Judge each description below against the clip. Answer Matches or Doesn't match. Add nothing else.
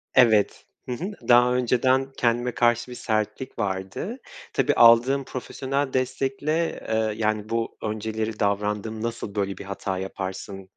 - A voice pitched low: Matches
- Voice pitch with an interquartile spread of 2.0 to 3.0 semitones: Doesn't match